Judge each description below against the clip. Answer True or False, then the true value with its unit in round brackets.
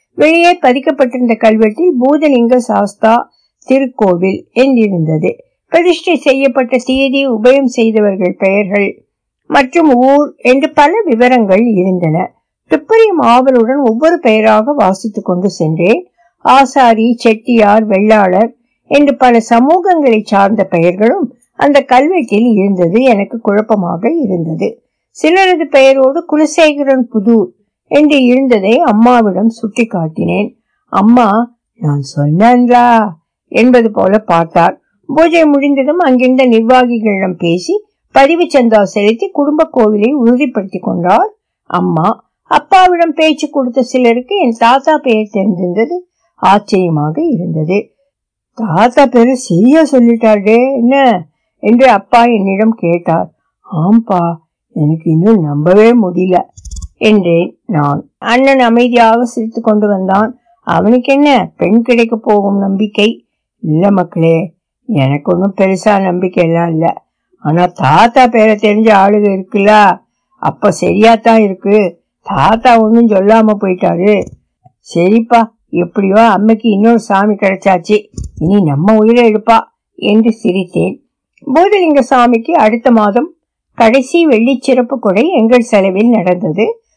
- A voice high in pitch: True (225 Hz)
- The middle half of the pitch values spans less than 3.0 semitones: False (4.7 semitones)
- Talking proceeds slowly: False (100 wpm)